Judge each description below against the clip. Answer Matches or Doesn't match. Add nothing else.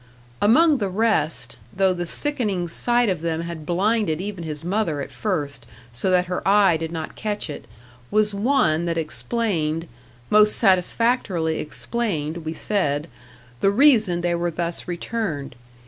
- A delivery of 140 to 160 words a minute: Matches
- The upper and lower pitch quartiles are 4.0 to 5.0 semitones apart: Matches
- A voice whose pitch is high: Doesn't match